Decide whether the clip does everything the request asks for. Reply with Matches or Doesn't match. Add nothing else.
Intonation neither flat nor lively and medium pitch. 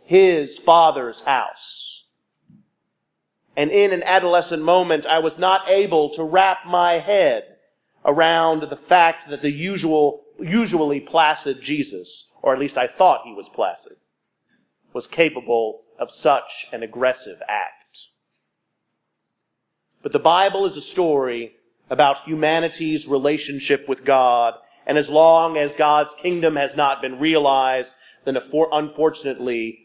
Matches